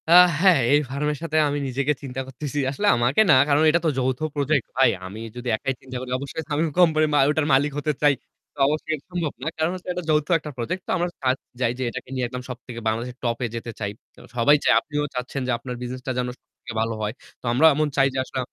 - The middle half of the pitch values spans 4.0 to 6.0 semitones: No, average, 3.4 semitones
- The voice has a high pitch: No, medium, 140 Hz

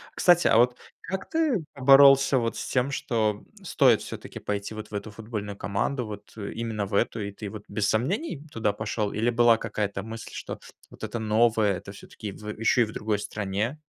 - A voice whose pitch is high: No, low, 110 Hz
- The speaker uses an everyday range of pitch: Yes, average, 3.0 semitones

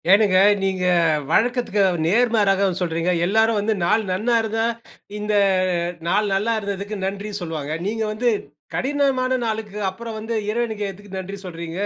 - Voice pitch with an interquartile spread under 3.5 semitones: Yes, average, 2.7 semitones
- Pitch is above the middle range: Yes, high, 210 Hz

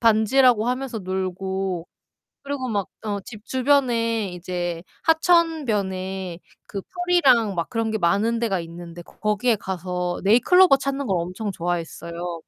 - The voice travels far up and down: Yes, wide, 5.7 semitones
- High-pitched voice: Yes, high, 210 Hz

